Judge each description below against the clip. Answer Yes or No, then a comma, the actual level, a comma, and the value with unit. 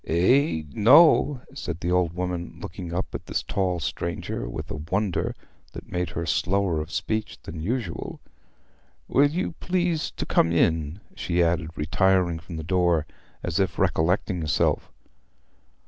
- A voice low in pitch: Yes, very low, 90 Hz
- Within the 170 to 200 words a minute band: No, average, 145 wpm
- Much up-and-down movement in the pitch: No, average, 4.0 semitones